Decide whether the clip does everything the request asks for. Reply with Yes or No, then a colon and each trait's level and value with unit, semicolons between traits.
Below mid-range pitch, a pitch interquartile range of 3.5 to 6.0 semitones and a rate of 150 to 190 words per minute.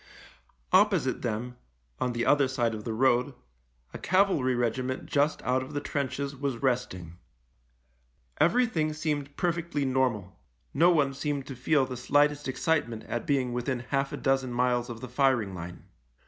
No: low, 130 Hz; average, 3.0 semitones; average, 160 wpm